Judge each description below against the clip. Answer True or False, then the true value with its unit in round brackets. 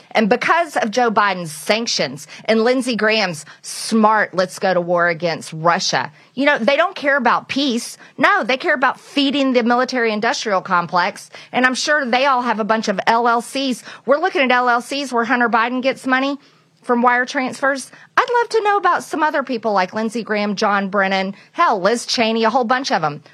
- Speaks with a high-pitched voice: True (235 Hz)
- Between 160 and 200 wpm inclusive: True (195 wpm)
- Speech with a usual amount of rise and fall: True (4.8 semitones)